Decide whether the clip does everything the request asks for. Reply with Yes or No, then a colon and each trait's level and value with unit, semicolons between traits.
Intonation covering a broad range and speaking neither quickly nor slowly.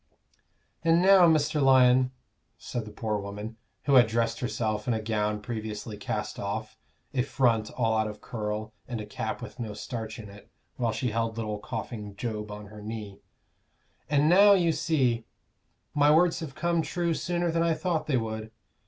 Yes: wide, 5.7 semitones; average, 180 wpm